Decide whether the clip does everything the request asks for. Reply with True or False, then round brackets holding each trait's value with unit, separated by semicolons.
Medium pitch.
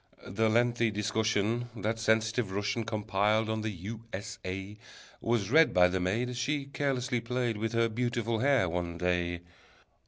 False (110 Hz)